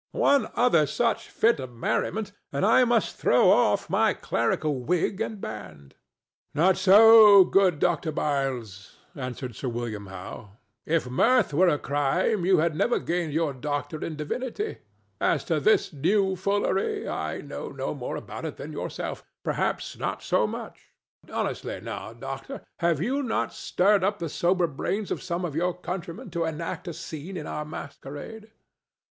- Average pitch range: No, wide, 6.2 semitones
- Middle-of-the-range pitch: Yes, medium, 165 Hz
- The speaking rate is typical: Yes, average, 160 wpm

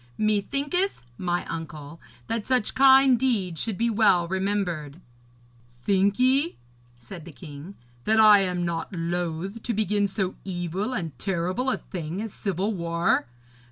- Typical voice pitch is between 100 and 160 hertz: No, high, 190 Hz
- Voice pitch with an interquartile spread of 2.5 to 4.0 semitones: No, average, 4.5 semitones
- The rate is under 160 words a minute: Yes, average, 140 wpm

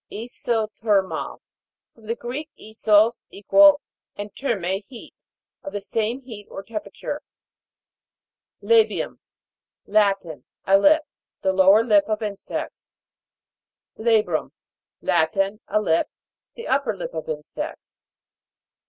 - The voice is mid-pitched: No, high, 215 Hz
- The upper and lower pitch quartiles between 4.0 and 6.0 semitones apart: No, average, 3.3 semitones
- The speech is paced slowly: Yes, slow, 110 wpm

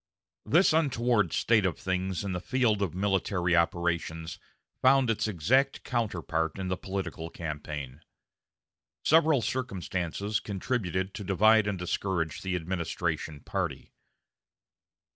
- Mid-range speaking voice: No, very low, 95 Hz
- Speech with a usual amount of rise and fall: Yes, average, 4.5 semitones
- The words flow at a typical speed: No, slow, 115 wpm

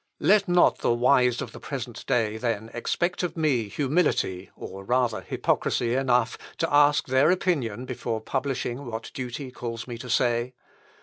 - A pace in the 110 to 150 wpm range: No, average, 160 wpm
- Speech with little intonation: No, average, 3.4 semitones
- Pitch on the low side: Yes, low, 125 Hz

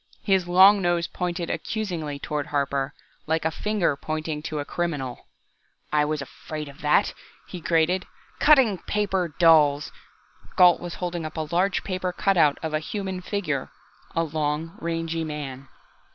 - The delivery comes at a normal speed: Yes, average, 150 wpm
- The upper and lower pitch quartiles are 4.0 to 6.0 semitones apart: No, average, 3.3 semitones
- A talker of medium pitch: Yes, medium, 165 Hz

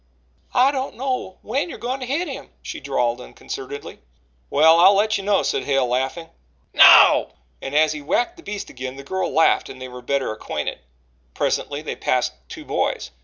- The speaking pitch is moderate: Yes, medium, 165 Hz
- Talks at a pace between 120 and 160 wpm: No, average, 185 wpm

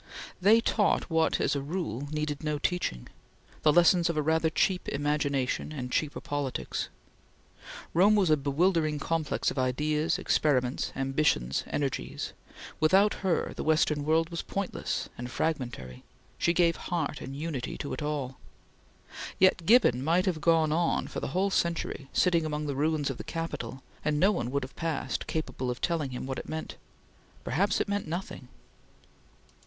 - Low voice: No, medium, 155 Hz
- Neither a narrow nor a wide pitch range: Yes, average, 3.6 semitones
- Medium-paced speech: Yes, average, 160 wpm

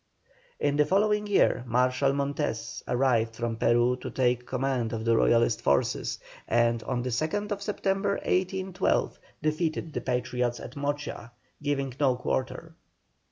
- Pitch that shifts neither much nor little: Yes, average, 4.7 semitones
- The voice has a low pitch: Yes, low, 130 Hz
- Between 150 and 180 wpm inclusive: No, slow, 135 wpm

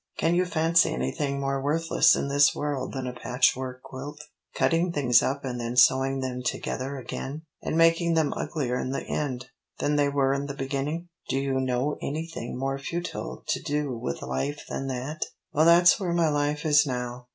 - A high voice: No, medium, 140 Hz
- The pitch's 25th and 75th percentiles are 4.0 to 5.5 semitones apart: No, average, 2.9 semitones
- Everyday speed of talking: Yes, average, 185 wpm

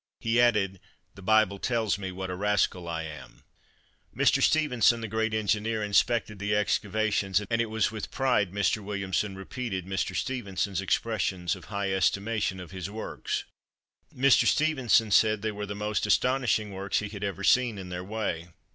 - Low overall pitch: Yes, low, 105 Hz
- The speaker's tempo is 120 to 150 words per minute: No, average, 165 wpm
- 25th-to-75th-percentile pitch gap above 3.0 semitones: No, narrow, 2.6 semitones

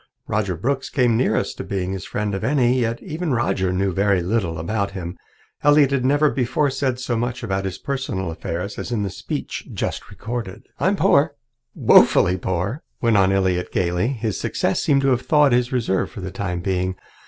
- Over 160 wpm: Yes, average, 190 wpm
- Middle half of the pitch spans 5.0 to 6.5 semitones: Yes, wide, 5.5 semitones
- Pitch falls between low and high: No, low, 110 Hz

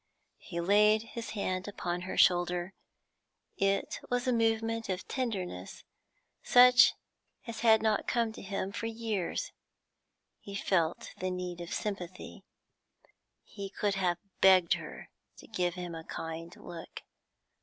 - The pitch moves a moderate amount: Yes, average, 3.9 semitones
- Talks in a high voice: Yes, high, 195 Hz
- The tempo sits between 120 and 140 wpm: Yes, slow, 135 wpm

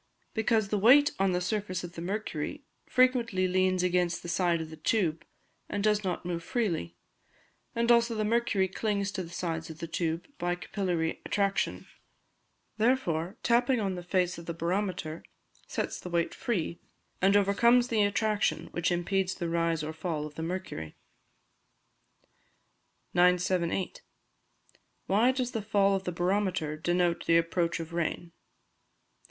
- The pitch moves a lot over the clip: No, average, 3.7 semitones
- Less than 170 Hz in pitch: No, medium, 185 Hz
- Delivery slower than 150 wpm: No, average, 155 wpm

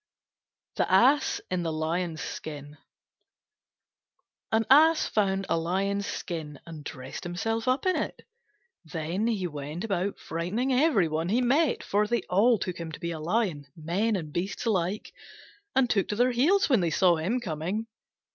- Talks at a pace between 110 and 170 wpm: Yes, average, 165 wpm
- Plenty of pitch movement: Yes, wide, 5.7 semitones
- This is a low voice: No, high, 190 Hz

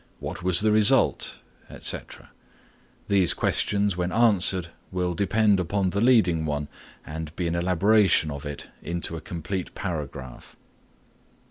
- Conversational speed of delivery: No, slow, 130 wpm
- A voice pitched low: Yes, very low, 90 Hz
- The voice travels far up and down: No, average, 3.7 semitones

